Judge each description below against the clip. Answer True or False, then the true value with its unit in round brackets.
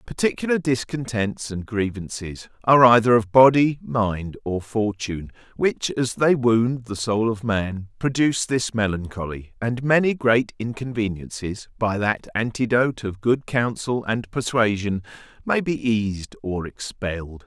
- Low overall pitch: True (115 Hz)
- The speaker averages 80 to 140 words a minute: True (135 wpm)